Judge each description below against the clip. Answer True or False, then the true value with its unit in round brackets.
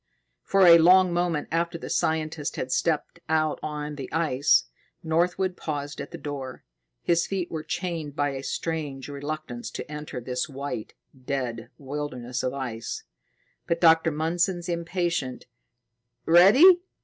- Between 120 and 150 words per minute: True (135 wpm)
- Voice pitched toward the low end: False (155 Hz)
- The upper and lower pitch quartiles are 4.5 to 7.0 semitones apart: False (3.5 semitones)